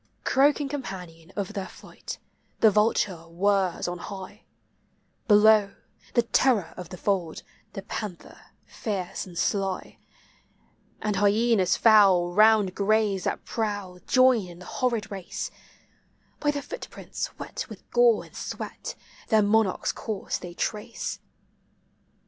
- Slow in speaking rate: Yes, slow, 125 wpm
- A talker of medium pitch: No, high, 205 Hz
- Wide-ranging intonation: No, average, 3.1 semitones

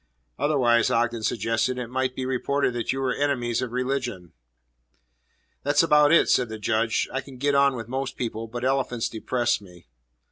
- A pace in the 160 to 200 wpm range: Yes, average, 175 wpm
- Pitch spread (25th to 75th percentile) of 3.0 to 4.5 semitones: No, narrow, 2.6 semitones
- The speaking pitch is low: Yes, low, 125 Hz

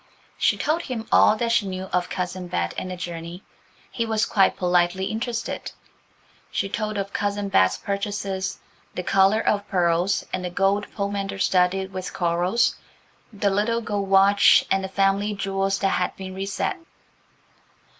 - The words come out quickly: No, average, 155 wpm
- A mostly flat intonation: Yes, narrow, 1.9 semitones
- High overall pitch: Yes, high, 195 Hz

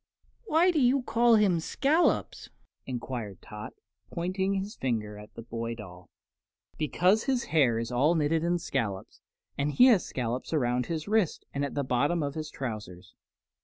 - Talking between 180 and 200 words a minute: No, average, 165 wpm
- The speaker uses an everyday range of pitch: No, wide, 8.6 semitones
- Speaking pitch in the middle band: Yes, medium, 145 Hz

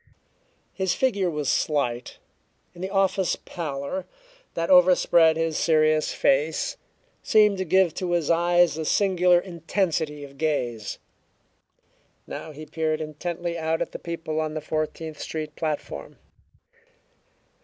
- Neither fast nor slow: No, slow, 125 wpm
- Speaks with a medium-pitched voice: Yes, medium, 160 Hz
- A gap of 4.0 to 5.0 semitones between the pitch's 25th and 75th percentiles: No, narrow, 2.4 semitones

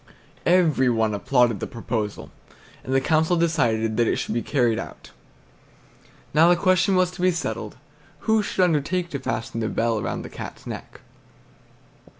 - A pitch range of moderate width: No, wide, 7.2 semitones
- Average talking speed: Yes, average, 160 wpm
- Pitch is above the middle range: No, low, 135 Hz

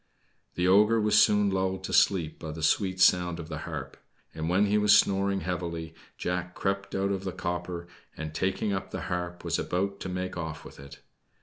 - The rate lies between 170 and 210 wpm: Yes, average, 200 wpm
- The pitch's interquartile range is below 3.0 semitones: Yes, narrow, 2.5 semitones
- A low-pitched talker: Yes, very low, 90 Hz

